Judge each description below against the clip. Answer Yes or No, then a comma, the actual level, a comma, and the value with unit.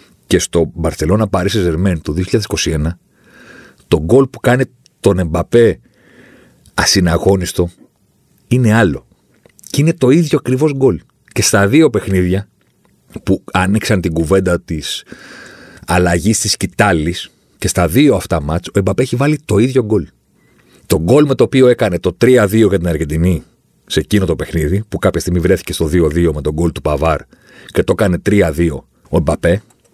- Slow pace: No, average, 155 wpm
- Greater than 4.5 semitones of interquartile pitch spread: Yes, average, 5.3 semitones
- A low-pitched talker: Yes, very low, 95 Hz